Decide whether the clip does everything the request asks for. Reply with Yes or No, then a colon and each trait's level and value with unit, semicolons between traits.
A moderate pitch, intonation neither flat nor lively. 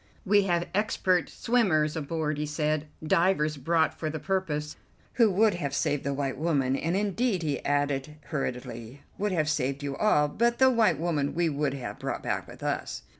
Yes: medium, 155 Hz; average, 4.6 semitones